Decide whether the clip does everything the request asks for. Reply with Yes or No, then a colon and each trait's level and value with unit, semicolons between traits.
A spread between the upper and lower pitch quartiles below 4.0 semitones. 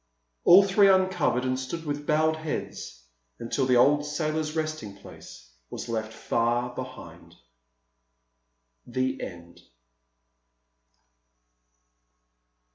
No: average, 4.7 semitones